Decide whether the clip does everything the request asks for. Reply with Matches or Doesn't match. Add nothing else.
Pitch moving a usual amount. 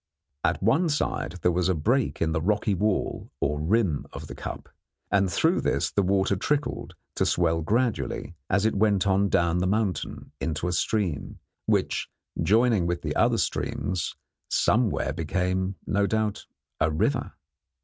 Matches